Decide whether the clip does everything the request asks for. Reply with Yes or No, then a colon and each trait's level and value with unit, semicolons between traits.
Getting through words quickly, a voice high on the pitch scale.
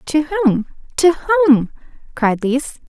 No: slow, 125 wpm; very high, 295 Hz